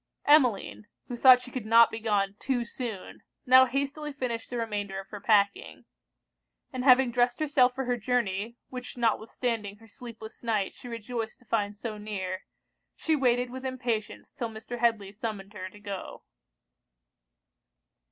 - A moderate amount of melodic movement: Yes, average, 3.3 semitones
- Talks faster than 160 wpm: No, average, 155 wpm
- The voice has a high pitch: Yes, high, 230 Hz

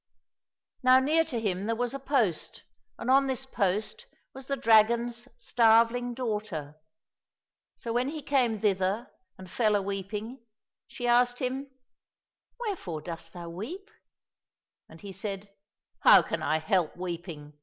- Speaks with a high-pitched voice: Yes, high, 230 Hz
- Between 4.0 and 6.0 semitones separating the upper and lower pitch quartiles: Yes, average, 5.3 semitones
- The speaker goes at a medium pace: Yes, average, 155 wpm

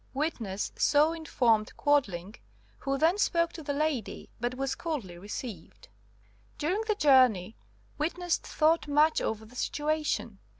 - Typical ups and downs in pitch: No, wide, 6.1 semitones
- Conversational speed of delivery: No, slow, 130 wpm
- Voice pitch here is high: Yes, very high, 285 Hz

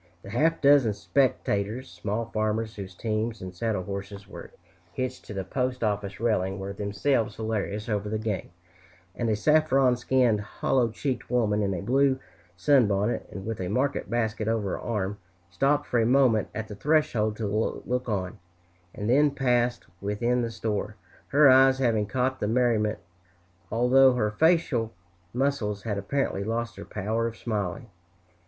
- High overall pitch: No, low, 115 Hz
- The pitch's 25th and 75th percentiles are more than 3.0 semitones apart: Yes, average, 3.5 semitones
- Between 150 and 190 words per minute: Yes, average, 160 wpm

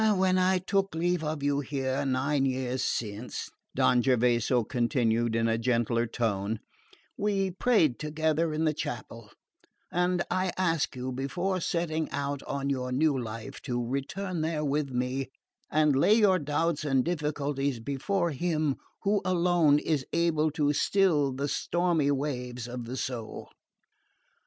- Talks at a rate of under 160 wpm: Yes, average, 145 wpm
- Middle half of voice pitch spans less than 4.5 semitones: No, average, 4.9 semitones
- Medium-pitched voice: Yes, medium, 145 Hz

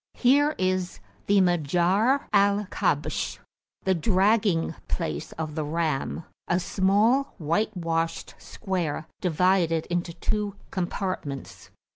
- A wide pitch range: No, average, 3.6 semitones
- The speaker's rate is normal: No, slow, 105 wpm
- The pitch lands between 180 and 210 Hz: Yes, medium, 185 Hz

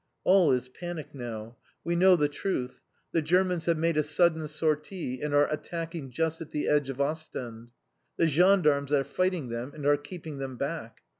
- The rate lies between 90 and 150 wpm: No, average, 180 wpm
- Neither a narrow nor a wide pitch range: Yes, average, 3.6 semitones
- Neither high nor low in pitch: Yes, medium, 150 Hz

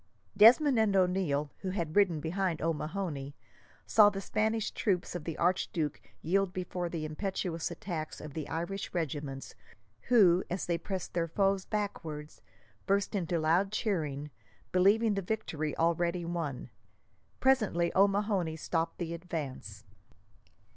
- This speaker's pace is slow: Yes, slow, 130 wpm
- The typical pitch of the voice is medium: Yes, medium, 175 Hz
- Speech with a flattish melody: No, average, 3.8 semitones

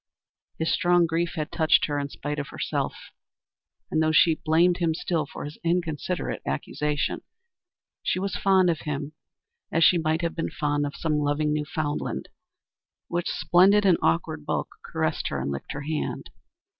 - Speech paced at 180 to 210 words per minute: No, average, 165 wpm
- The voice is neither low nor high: Yes, medium, 160 Hz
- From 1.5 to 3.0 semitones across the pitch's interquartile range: Yes, average, 2.7 semitones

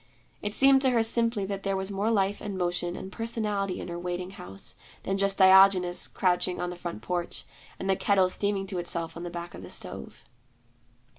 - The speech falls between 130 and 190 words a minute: No, fast, 205 wpm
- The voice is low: No, high, 190 Hz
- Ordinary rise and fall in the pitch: No, narrow, 2.3 semitones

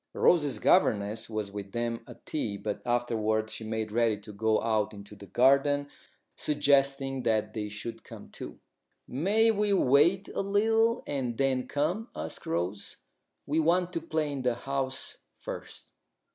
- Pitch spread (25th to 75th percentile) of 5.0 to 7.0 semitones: Yes, wide, 5.6 semitones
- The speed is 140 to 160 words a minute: Yes, average, 155 wpm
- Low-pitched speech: Yes, low, 125 Hz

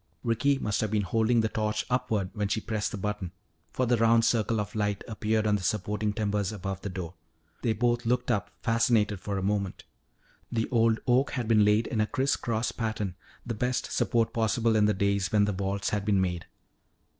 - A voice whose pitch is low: Yes, low, 110 Hz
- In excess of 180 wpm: Yes, average, 200 wpm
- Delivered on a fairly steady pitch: Yes, narrow, 2.1 semitones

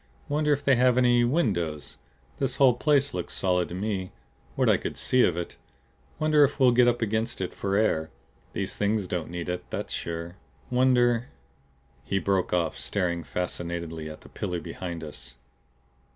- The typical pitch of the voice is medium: No, very low, 95 Hz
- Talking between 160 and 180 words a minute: Yes, average, 175 wpm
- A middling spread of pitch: No, wide, 6.3 semitones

